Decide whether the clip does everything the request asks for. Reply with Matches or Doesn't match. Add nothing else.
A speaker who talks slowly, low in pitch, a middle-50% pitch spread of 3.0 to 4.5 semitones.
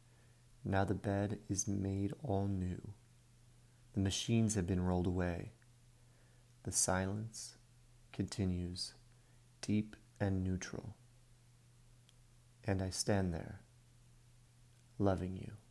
Matches